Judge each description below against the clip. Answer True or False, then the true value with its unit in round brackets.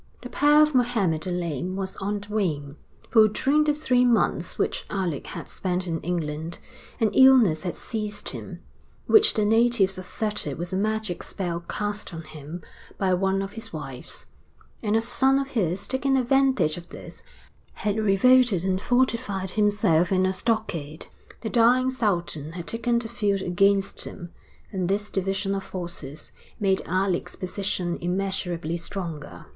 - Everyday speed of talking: True (160 wpm)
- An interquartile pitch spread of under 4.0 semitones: False (4.4 semitones)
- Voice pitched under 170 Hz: False (195 Hz)